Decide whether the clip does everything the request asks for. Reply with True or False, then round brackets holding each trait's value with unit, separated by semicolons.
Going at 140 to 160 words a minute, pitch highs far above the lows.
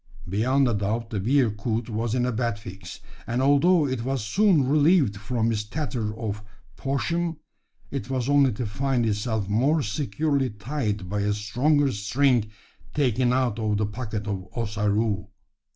False (155 wpm; 4.5 semitones)